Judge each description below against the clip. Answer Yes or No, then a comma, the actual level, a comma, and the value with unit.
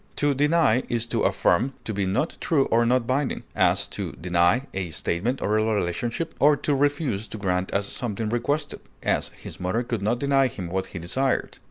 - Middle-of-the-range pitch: No, low, 115 Hz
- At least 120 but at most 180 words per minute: No, average, 195 wpm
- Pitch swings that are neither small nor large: No, wide, 5.9 semitones